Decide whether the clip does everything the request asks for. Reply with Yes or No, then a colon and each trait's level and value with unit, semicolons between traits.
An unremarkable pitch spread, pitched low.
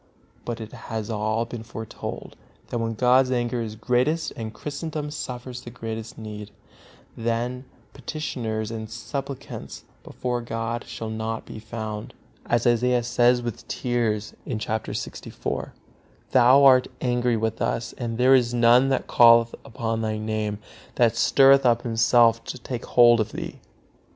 No: narrow, 1.9 semitones; low, 120 Hz